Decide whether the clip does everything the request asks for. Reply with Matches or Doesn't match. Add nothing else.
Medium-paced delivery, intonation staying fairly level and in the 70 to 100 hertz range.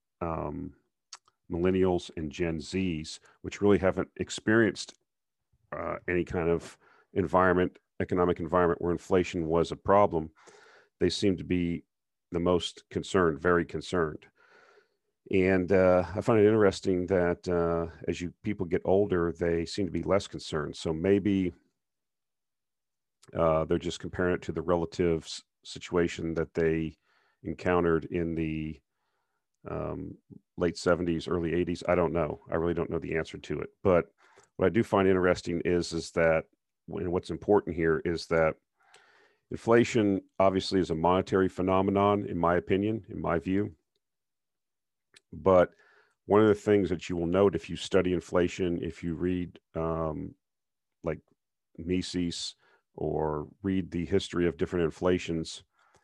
Matches